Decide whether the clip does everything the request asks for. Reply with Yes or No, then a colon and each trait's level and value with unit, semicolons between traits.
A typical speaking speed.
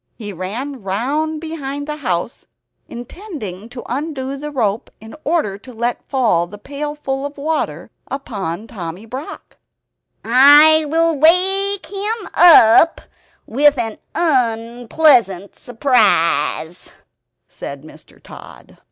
No: slow, 110 wpm